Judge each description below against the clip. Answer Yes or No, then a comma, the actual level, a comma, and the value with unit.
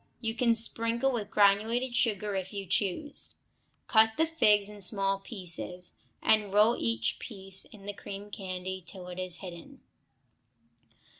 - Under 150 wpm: Yes, average, 140 wpm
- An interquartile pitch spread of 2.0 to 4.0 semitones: Yes, average, 3.0 semitones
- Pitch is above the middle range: Yes, high, 205 Hz